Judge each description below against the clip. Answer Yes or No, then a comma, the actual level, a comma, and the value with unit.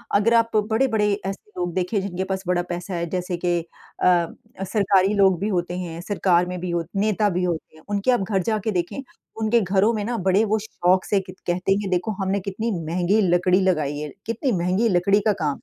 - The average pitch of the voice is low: No, high, 190 Hz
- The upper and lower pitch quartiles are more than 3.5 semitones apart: No, average, 2.9 semitones